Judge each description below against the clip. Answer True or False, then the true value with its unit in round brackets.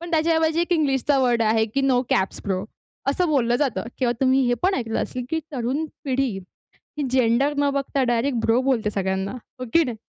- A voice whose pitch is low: False (260 Hz)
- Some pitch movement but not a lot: True (3.6 semitones)